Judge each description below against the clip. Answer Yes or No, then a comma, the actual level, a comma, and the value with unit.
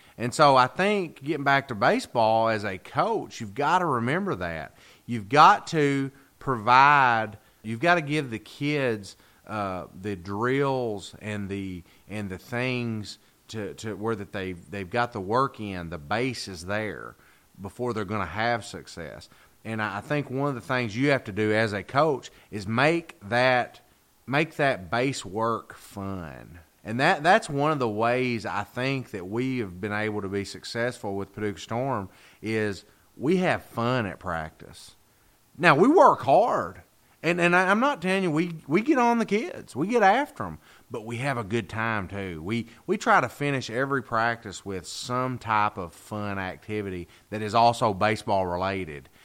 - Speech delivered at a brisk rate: No, average, 180 wpm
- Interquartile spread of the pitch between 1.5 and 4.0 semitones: No, average, 4.7 semitones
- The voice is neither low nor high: No, low, 110 Hz